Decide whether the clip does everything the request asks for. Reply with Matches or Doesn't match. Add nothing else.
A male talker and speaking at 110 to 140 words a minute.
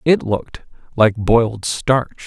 Matches